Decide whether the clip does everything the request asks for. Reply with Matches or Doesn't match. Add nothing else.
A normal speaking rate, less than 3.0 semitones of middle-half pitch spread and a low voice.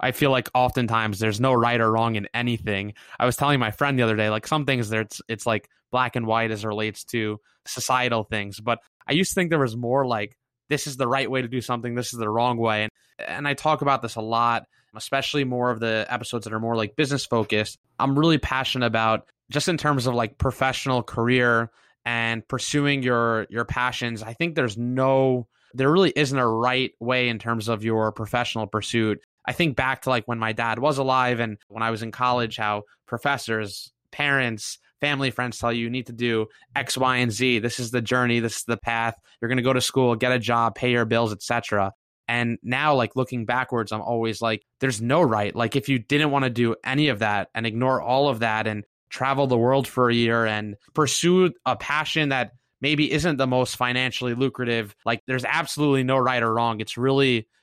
Doesn't match